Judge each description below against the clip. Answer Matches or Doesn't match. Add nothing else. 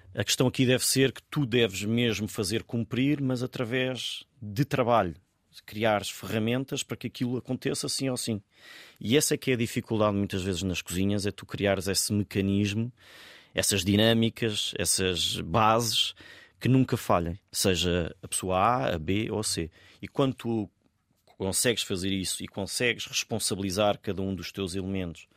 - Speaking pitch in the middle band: Doesn't match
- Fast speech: Doesn't match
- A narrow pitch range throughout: Doesn't match